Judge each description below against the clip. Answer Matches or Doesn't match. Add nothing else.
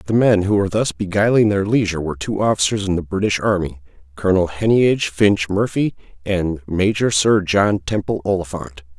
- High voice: Doesn't match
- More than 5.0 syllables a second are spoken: Matches